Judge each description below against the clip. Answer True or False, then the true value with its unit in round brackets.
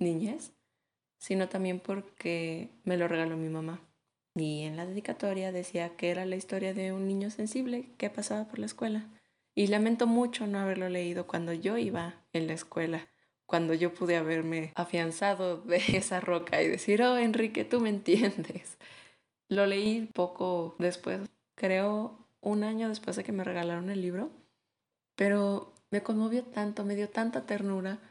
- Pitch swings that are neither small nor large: True (3.5 semitones)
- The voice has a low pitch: False (190 Hz)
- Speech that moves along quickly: False (160 wpm)